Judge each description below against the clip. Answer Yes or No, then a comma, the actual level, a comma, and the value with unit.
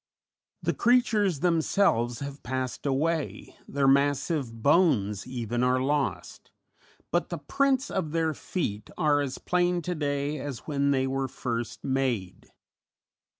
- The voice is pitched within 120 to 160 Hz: Yes, medium, 140 Hz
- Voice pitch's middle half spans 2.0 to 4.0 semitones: No, average, 4.5 semitones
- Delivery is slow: Yes, slow, 130 wpm